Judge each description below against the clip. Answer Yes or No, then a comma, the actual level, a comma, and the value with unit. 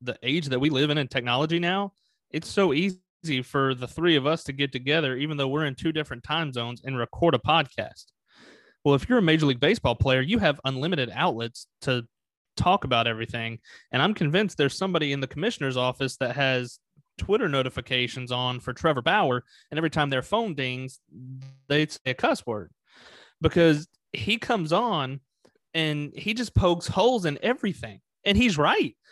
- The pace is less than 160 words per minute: No, average, 185 wpm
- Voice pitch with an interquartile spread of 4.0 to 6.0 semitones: Yes, average, 4.3 semitones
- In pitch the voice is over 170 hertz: No, medium, 140 Hz